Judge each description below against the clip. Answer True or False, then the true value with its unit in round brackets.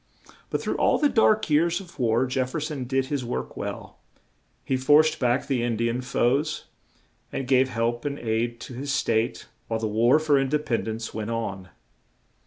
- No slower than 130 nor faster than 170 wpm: False (195 wpm)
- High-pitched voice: False (130 Hz)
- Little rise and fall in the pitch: False (3.9 semitones)